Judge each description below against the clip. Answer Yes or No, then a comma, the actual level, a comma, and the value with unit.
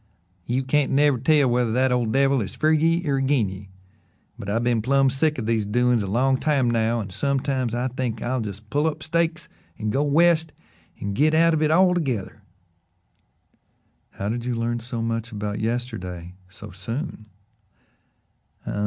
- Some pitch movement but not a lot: Yes, average, 4.5 semitones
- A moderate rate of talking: Yes, average, 170 wpm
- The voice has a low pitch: Yes, low, 125 Hz